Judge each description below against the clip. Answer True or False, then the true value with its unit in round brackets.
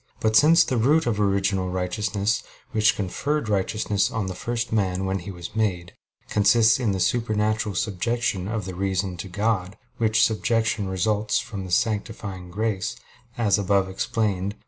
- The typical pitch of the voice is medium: False (105 Hz)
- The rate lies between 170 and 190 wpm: False (155 wpm)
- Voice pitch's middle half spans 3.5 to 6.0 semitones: False (2.8 semitones)